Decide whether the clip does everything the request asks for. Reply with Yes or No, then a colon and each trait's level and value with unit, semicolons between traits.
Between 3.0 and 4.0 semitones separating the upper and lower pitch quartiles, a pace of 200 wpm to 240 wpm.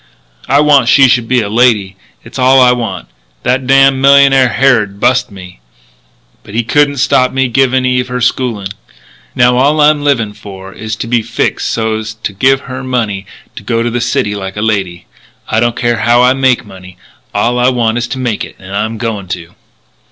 Yes: average, 3.5 semitones; fast, 205 wpm